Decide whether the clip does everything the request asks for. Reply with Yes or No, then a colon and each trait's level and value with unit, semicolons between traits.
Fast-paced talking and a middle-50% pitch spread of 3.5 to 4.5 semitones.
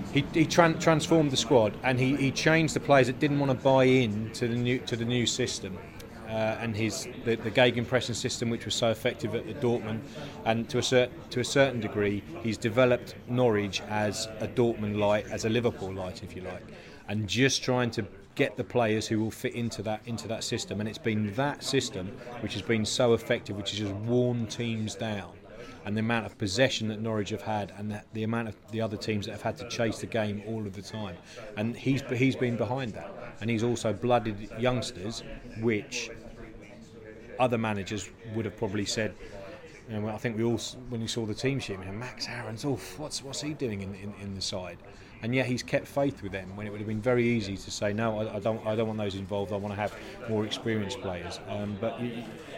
No: fast, 225 wpm; average, 2.8 semitones